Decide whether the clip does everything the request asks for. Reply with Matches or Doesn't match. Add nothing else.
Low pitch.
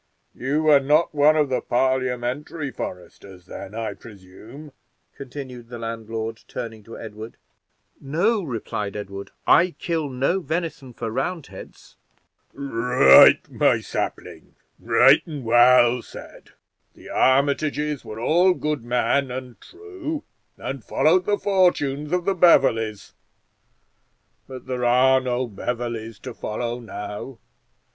Matches